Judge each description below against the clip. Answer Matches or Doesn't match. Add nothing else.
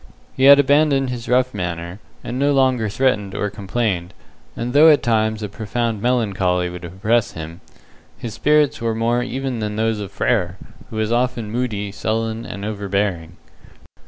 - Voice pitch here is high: Doesn't match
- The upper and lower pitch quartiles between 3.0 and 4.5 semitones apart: Matches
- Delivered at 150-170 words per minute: Matches